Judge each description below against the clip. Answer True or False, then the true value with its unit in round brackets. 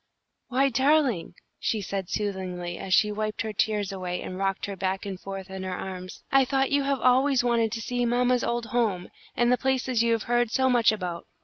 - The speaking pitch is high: True (220 Hz)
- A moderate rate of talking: False (210 wpm)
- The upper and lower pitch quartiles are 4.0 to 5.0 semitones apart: True (4.6 semitones)